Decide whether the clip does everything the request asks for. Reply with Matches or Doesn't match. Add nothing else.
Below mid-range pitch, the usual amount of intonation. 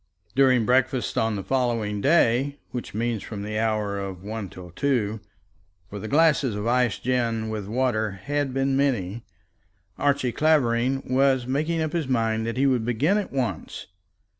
Matches